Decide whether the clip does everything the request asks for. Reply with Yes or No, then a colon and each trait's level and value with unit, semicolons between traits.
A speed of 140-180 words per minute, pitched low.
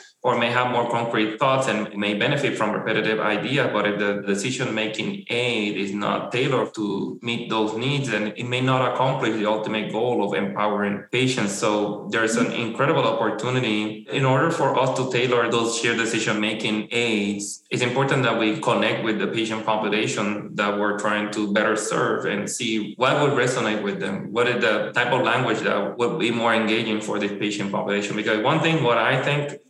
No: average, 190 wpm; low, 110 Hz